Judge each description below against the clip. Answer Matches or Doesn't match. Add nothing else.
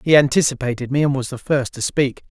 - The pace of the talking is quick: Matches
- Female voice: Doesn't match